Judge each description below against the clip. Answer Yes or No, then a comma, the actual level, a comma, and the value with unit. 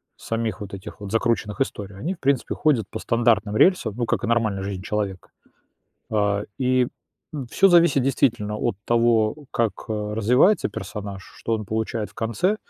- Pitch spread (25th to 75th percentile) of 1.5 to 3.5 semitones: Yes, average, 3.2 semitones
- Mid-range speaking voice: No, low, 110 Hz